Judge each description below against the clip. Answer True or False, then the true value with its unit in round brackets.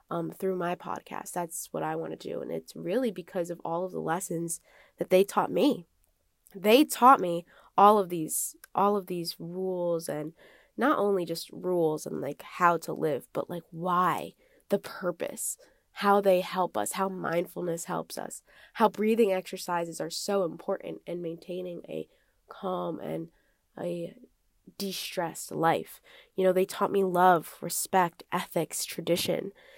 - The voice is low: False (180 Hz)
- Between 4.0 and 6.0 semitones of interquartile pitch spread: False (2.8 semitones)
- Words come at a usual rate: True (160 wpm)